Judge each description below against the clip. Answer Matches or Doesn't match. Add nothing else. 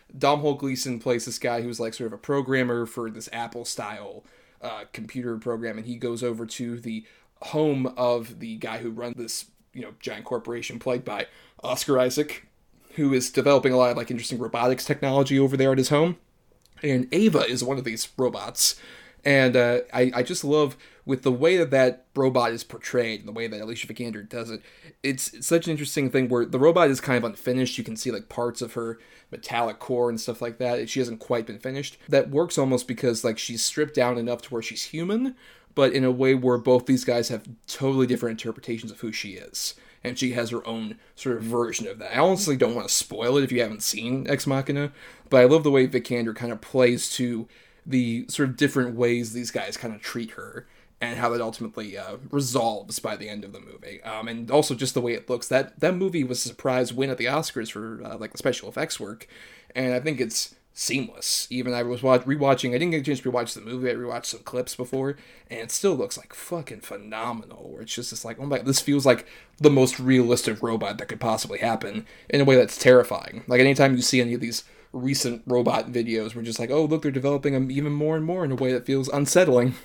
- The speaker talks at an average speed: Doesn't match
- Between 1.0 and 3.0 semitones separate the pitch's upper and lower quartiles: Matches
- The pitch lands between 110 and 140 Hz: Matches